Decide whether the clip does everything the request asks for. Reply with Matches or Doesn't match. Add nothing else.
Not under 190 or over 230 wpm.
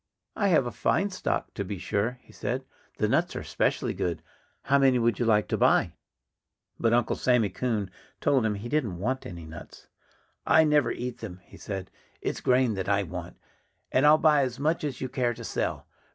Matches